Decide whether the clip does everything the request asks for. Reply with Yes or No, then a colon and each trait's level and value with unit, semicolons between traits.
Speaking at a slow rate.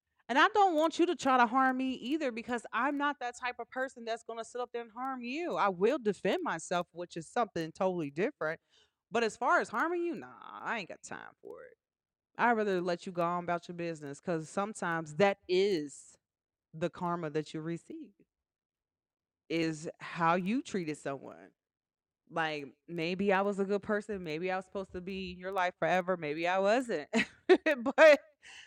No: average, 195 wpm